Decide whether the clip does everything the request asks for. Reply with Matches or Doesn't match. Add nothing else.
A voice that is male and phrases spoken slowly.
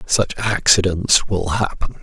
Matches